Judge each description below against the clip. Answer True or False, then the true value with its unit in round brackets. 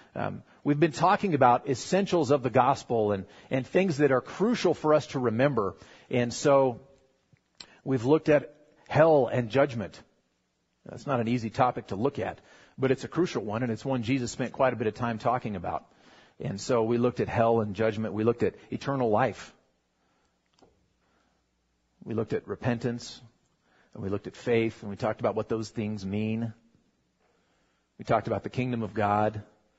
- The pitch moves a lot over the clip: False (3.9 semitones)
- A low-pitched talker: True (120 Hz)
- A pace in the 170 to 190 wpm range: True (180 wpm)